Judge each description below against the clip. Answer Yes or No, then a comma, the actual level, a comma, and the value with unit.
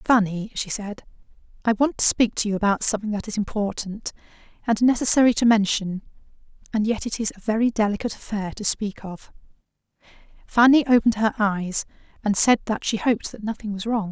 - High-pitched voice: Yes, high, 215 Hz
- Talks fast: No, average, 180 wpm